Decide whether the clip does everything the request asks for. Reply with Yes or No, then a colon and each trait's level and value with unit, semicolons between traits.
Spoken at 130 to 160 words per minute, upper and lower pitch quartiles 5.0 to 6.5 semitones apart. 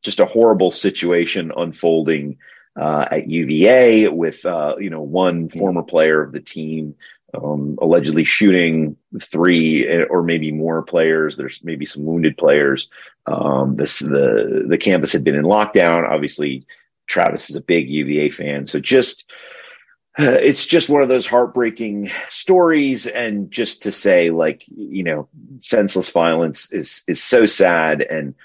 Yes: average, 150 wpm; wide, 5.5 semitones